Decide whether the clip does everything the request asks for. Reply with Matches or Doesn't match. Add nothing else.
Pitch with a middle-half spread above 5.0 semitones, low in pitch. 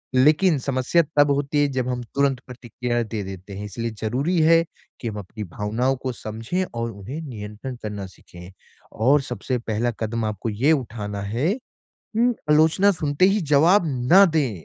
Matches